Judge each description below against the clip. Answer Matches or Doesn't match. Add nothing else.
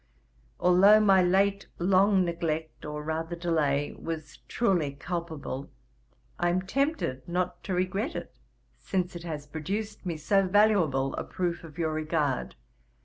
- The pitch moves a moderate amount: Matches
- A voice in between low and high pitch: Matches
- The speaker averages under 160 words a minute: Matches